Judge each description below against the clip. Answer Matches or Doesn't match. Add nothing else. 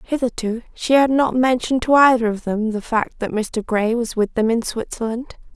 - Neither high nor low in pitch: Doesn't match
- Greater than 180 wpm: Matches